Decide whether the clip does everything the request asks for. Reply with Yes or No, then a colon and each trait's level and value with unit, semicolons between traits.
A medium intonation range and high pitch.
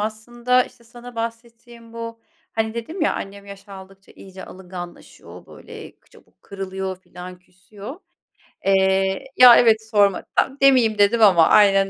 Yes: average, 3.4 semitones; high, 215 Hz